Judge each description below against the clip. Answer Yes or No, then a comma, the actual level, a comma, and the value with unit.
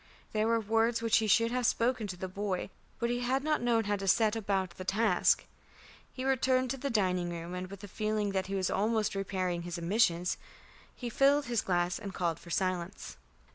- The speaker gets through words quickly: Yes, fast, 210 wpm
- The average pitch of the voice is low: No, high, 205 Hz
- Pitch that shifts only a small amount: No, average, 3.9 semitones